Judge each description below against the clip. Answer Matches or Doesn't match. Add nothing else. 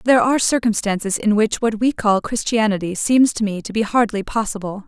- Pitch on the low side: Doesn't match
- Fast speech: Doesn't match